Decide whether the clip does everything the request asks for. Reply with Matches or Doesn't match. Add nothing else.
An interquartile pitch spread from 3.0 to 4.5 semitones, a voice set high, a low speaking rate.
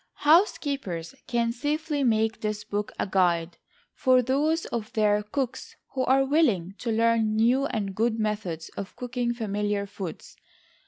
Doesn't match